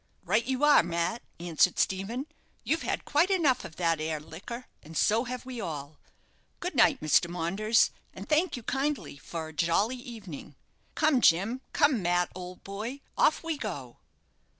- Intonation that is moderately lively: No, wide, 7.4 semitones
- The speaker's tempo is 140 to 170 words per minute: Yes, average, 165 wpm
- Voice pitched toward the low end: No, high, 210 Hz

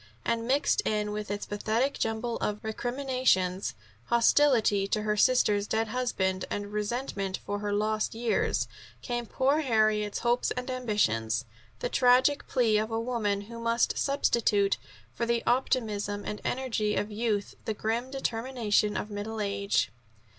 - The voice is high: Yes, high, 220 Hz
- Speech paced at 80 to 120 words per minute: No, average, 145 wpm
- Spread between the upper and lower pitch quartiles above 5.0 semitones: No, average, 2.8 semitones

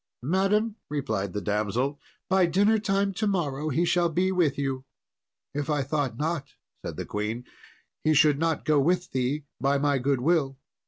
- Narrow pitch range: No, average, 4.6 semitones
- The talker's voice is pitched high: No, medium, 150 Hz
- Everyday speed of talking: Yes, average, 165 wpm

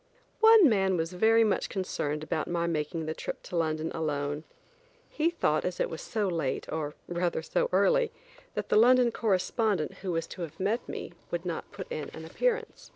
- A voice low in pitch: No, medium, 175 Hz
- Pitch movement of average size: No, wide, 5.9 semitones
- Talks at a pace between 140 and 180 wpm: No, average, 190 wpm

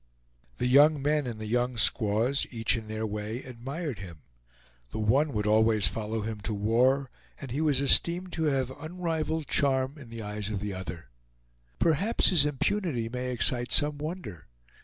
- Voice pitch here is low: Yes, low, 125 Hz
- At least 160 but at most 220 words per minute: Yes, average, 170 wpm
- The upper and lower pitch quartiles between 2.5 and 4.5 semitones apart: No, average, 5.2 semitones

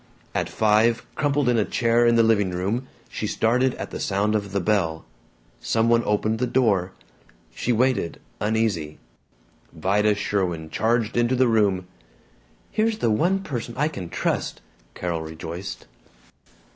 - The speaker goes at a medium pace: Yes, average, 145 wpm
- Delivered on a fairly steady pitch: No, average, 3.7 semitones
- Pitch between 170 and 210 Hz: No, low, 110 Hz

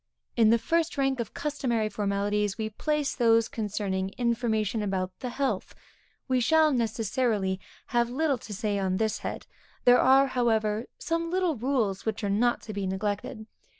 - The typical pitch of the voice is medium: No, high, 225 Hz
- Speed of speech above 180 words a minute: No, average, 165 wpm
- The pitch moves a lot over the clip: No, average, 4.0 semitones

